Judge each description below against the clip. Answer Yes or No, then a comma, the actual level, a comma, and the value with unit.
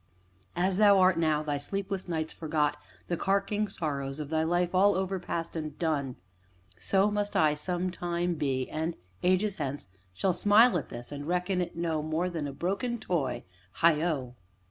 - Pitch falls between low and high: Yes, medium, 170 Hz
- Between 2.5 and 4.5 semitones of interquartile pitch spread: Yes, average, 3.8 semitones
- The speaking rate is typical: Yes, average, 165 wpm